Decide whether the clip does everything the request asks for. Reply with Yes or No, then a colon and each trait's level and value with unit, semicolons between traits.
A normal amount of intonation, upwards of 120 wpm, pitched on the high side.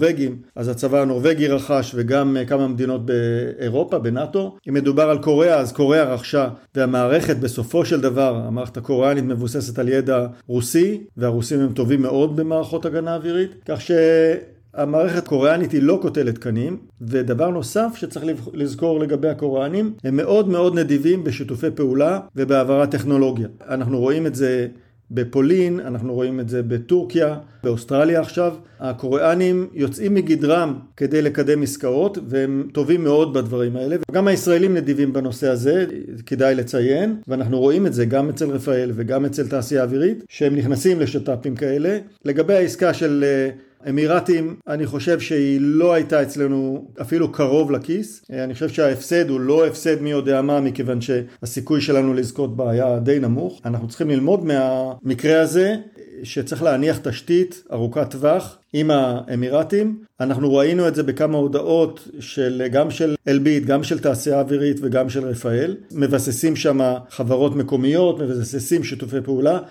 No: average, 3.5 semitones; average, 140 wpm; medium, 140 Hz